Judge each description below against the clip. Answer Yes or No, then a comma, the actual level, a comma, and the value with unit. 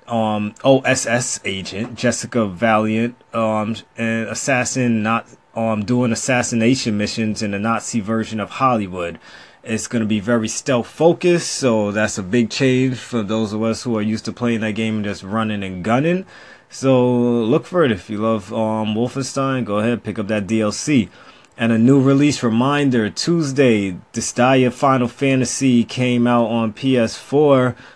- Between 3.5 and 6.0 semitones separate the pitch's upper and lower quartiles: No, narrow, 2.4 semitones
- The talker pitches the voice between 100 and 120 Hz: Yes, low, 115 Hz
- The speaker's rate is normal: Yes, average, 160 wpm